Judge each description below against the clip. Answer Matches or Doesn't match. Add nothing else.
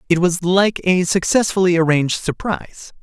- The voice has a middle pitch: Matches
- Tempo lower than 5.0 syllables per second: Doesn't match